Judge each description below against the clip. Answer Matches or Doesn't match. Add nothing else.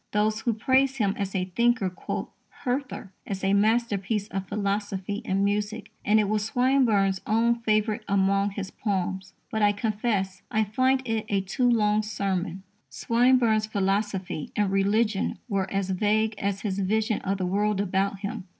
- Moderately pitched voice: Doesn't match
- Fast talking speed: Doesn't match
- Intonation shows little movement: Matches